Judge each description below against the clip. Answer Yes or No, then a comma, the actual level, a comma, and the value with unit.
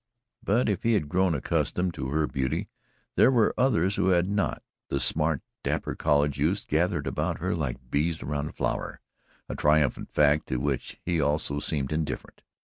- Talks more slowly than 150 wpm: No, average, 175 wpm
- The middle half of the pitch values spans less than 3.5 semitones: No, average, 4.2 semitones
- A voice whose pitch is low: Yes, very low, 75 Hz